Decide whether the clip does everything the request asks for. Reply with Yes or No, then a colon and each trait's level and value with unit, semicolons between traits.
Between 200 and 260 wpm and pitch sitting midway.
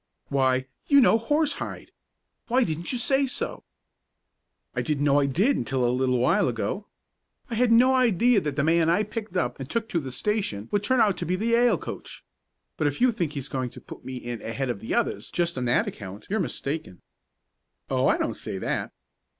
Yes: fast, 205 wpm; medium, 170 Hz